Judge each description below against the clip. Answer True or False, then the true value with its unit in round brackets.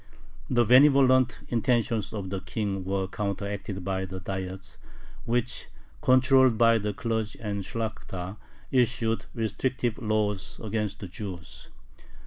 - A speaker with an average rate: False (115 wpm)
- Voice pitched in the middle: False (110 Hz)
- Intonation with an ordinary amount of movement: True (3.4 semitones)